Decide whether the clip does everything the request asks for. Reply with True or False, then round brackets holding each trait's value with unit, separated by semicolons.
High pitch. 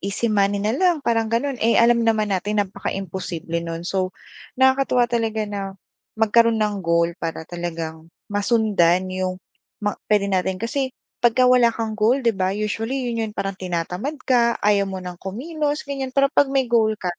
True (215 Hz)